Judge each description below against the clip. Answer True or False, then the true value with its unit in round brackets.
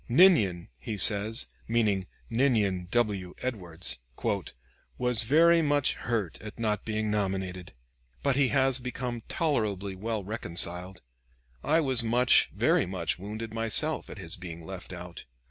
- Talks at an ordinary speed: False (130 wpm)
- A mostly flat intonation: False (4.8 semitones)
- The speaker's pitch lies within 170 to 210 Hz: False (110 Hz)